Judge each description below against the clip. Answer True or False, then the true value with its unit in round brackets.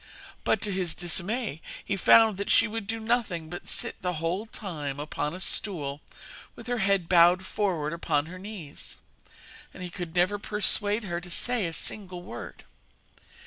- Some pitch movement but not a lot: True (3.6 semitones)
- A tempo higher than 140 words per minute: True (170 wpm)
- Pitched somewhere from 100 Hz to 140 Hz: False (185 Hz)